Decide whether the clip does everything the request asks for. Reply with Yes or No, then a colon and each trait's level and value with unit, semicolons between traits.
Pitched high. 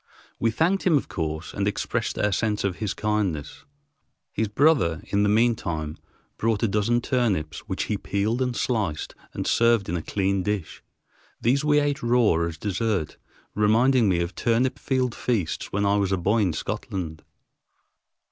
No: low, 105 Hz